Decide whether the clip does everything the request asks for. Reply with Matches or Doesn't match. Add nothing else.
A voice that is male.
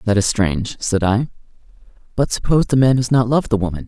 Matches